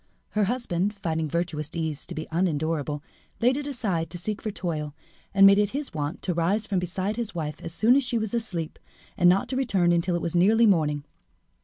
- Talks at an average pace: No, fast, 210 wpm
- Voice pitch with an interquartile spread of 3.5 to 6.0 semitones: Yes, average, 4.7 semitones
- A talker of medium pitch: Yes, medium, 180 Hz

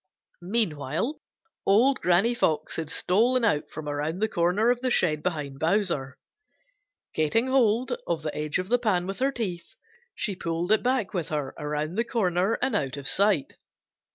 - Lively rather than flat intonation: Yes, wide, 6.9 semitones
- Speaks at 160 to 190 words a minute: Yes, average, 170 wpm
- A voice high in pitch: No, medium, 180 Hz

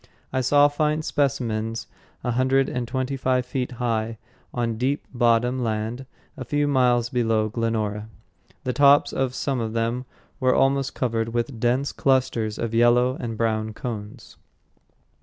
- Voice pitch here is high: No, low, 120 Hz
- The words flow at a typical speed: Yes, average, 145 wpm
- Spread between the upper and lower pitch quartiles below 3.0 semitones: Yes, narrow, 2.5 semitones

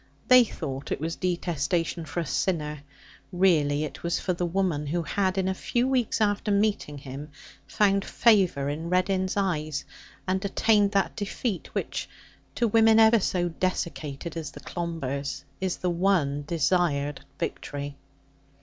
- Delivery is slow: No, average, 150 wpm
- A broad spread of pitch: No, average, 4.7 semitones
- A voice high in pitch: No, medium, 175 Hz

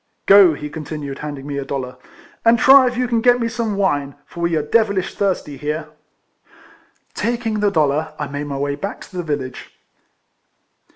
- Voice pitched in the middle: Yes, medium, 155 Hz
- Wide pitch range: Yes, wide, 6.5 semitones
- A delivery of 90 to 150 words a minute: No, average, 185 wpm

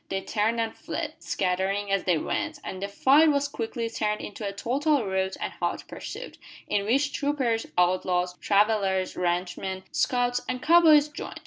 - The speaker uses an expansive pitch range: Yes, wide, 5.7 semitones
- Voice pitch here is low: No, high, 210 Hz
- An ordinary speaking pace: Yes, average, 175 wpm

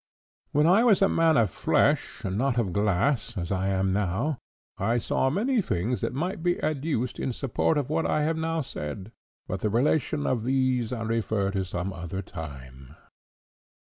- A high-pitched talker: No, low, 120 Hz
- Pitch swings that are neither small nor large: No, wide, 7.9 semitones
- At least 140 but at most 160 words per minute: No, average, 180 wpm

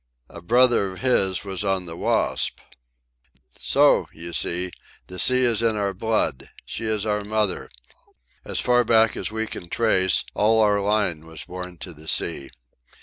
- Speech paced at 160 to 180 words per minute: Yes, average, 165 wpm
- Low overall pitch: Yes, low, 100 Hz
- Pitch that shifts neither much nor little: Yes, average, 3.7 semitones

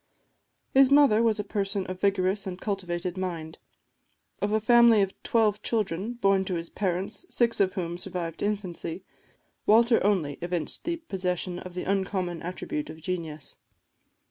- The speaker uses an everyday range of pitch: Yes, average, 3.2 semitones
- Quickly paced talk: No, average, 155 wpm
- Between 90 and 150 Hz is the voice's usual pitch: No, high, 190 Hz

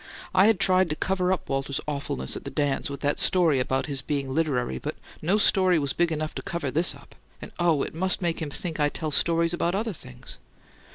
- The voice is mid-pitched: Yes, medium, 160 Hz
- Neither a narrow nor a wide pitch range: Yes, average, 4.2 semitones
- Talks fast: Yes, fast, 220 wpm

